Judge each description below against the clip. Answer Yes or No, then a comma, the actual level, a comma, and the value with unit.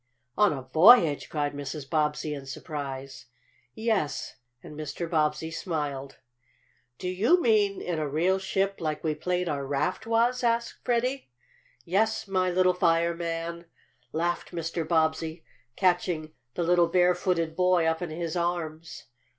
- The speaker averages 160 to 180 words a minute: No, average, 140 wpm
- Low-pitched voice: No, medium, 170 Hz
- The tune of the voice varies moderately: Yes, average, 3.1 semitones